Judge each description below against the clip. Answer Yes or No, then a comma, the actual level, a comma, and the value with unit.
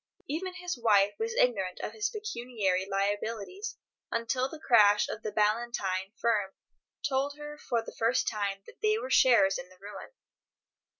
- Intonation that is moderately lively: No, wide, 5.8 semitones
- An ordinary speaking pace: Yes, average, 160 wpm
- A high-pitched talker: Yes, high, 230 Hz